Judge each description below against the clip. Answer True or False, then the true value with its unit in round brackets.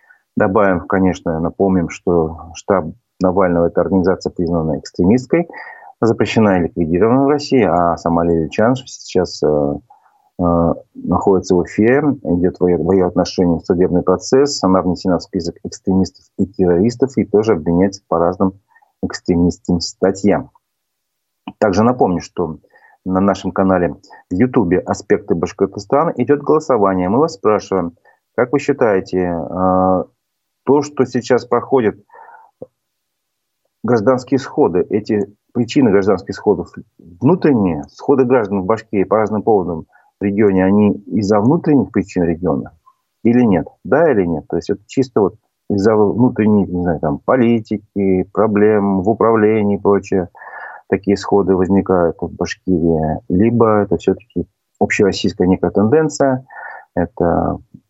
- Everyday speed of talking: True (130 wpm)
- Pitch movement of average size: True (4.1 semitones)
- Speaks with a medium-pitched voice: False (95 Hz)